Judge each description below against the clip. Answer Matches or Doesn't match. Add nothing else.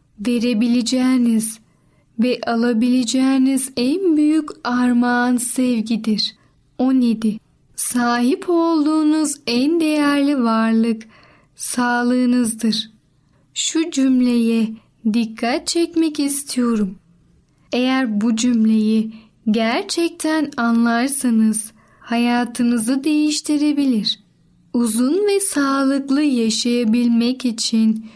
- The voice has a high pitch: Matches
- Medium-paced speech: Doesn't match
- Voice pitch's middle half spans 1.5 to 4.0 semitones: Matches